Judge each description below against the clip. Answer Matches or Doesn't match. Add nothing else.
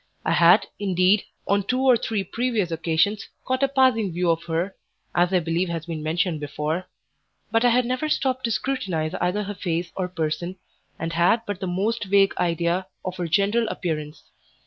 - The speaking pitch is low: Doesn't match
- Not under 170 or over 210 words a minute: Matches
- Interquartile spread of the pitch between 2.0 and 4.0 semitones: Doesn't match